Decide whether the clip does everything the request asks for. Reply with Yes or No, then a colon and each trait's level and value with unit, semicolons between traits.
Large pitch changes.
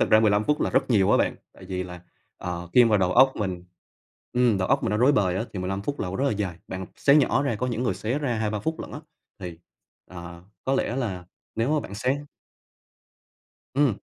Yes: wide, 5.8 semitones